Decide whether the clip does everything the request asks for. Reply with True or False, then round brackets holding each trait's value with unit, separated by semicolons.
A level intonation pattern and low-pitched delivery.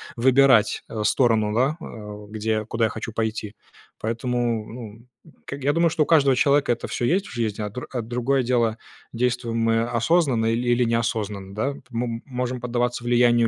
True (2.1 semitones; 120 Hz)